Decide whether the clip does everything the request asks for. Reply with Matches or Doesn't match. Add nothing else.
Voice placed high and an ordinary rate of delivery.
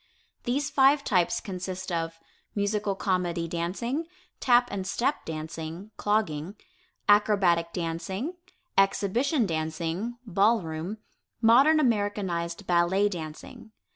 Doesn't match